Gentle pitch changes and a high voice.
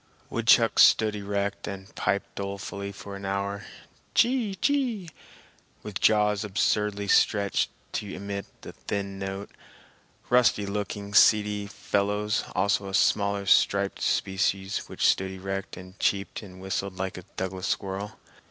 No: narrow, 1.1 semitones; low, 100 Hz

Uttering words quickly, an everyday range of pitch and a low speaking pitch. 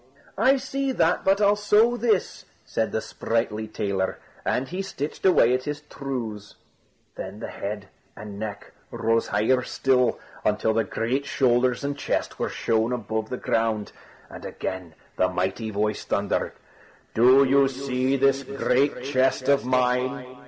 No: average, 150 wpm; average, 4.0 semitones; low, 125 Hz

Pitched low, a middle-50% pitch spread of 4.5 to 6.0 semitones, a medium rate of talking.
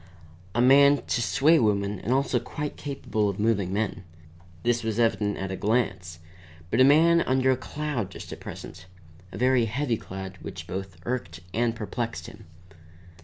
Yes: low, 115 Hz; average, 4.8 semitones; average, 170 wpm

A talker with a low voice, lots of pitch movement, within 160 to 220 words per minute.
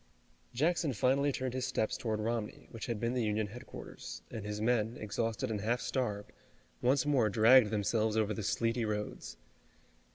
No: low, 115 Hz; average, 3.0 semitones; average, 165 wpm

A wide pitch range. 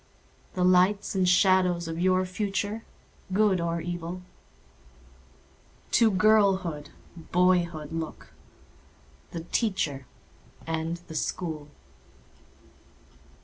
No: average, 3.5 semitones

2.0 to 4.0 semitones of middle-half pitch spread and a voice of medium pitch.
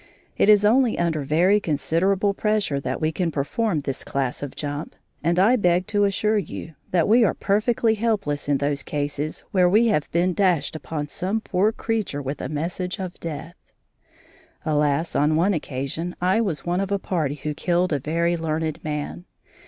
No: average, 5.0 semitones; medium, 170 Hz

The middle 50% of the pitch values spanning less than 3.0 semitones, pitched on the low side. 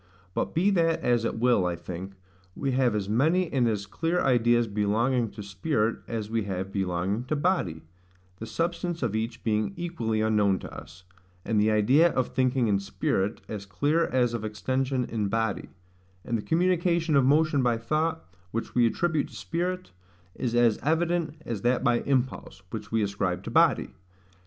No: wide, 5.6 semitones; low, 120 Hz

